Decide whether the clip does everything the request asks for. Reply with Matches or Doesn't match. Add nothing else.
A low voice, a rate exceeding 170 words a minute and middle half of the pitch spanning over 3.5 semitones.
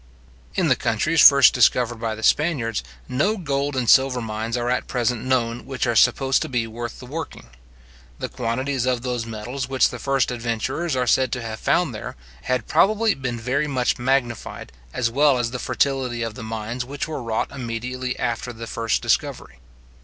Doesn't match